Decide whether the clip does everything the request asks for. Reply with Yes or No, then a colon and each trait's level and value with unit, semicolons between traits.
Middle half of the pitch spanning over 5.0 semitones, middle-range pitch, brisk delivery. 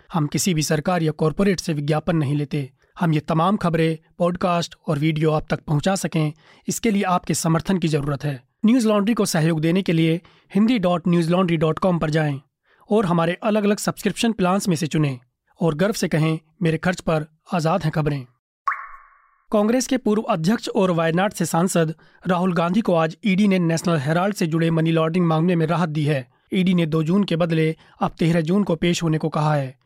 No: average, 2.8 semitones; medium, 170 Hz; fast, 205 wpm